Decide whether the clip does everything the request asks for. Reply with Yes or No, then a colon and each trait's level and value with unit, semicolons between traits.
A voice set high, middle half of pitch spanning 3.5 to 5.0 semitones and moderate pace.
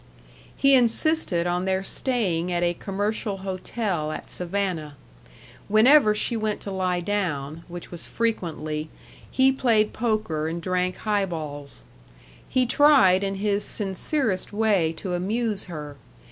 No: high, 195 Hz; average, 4.0 semitones; slow, 130 wpm